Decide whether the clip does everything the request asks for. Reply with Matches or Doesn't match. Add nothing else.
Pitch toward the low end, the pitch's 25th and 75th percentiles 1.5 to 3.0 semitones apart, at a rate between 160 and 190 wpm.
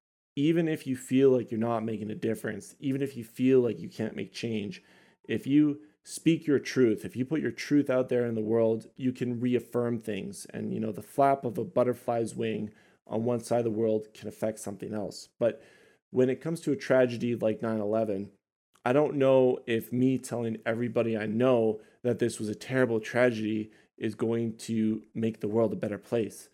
Doesn't match